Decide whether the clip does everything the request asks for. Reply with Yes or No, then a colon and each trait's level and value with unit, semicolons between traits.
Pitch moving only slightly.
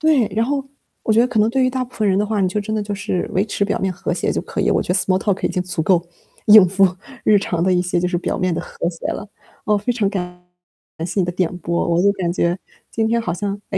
No: average, 3.3 semitones